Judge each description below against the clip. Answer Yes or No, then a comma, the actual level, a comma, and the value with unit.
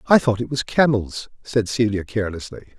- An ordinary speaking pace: Yes, average, 175 wpm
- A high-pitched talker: No, low, 115 Hz